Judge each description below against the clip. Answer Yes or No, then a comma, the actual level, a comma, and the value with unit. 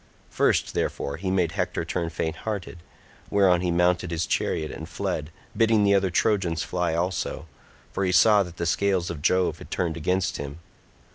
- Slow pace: No, average, 170 wpm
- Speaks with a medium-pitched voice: No, very low, 90 Hz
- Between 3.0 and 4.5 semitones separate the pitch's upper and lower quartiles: No, narrow, 2.5 semitones